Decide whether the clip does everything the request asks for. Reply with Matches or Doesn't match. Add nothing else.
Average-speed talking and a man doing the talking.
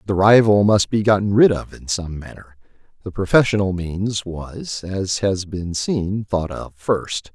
Matches